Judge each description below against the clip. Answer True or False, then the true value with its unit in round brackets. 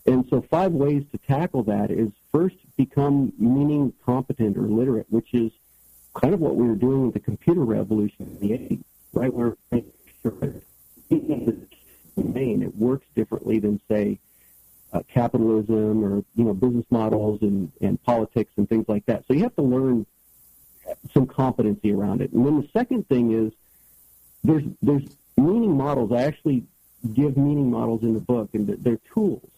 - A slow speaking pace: False (160 wpm)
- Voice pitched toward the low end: True (115 Hz)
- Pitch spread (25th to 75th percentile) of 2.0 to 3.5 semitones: False (4.1 semitones)